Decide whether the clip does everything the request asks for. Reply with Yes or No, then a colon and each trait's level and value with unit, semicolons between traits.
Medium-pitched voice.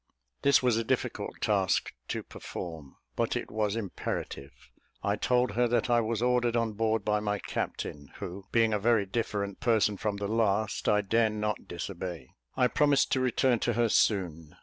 No: low, 110 Hz